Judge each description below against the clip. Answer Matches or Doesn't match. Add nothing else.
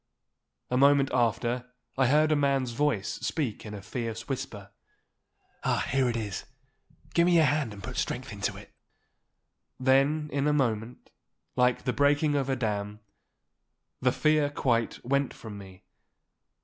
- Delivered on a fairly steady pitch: Doesn't match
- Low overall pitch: Matches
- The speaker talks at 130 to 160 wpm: Matches